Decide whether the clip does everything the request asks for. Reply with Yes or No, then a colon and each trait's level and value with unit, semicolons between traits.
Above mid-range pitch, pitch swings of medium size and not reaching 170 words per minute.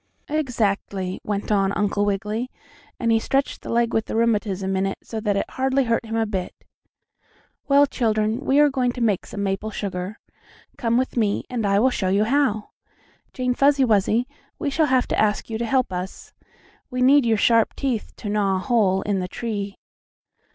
No: high, 220 Hz; average, 3.8 semitones; average, 190 wpm